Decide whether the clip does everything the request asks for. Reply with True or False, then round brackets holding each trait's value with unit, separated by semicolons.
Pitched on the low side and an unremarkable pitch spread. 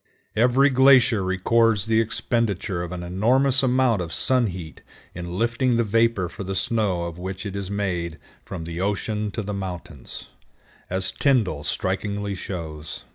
True (100 Hz; 4.3 semitones)